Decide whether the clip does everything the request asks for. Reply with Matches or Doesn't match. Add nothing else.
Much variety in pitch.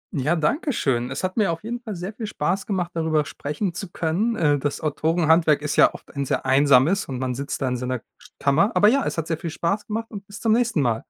Matches